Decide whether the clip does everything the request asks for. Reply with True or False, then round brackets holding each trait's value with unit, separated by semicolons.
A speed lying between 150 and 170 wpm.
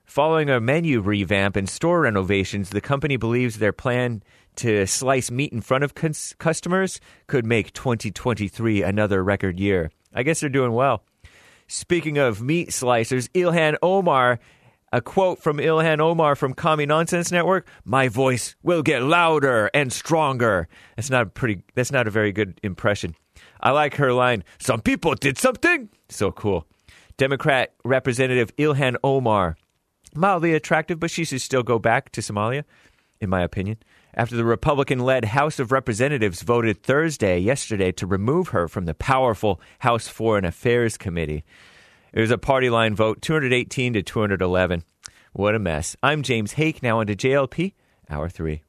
True (165 wpm)